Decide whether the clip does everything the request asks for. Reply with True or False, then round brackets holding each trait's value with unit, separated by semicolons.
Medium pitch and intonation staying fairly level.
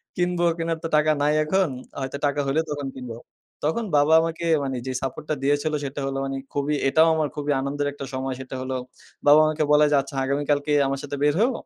True (145 Hz; 2.2 semitones)